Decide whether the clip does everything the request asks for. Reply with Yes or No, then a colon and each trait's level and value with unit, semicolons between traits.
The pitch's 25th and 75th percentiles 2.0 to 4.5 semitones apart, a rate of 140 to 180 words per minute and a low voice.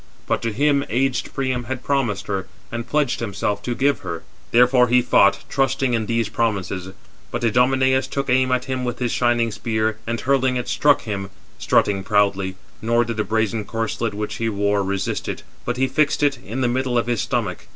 No: average, 3.5 semitones; average, 200 wpm; low, 120 Hz